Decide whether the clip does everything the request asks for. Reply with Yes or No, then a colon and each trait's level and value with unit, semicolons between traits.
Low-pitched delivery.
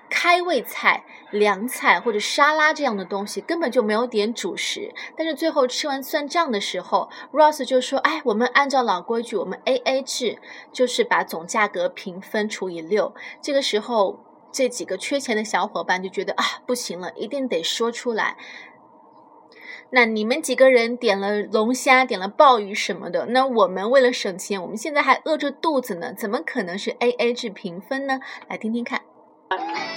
No: high, 245 Hz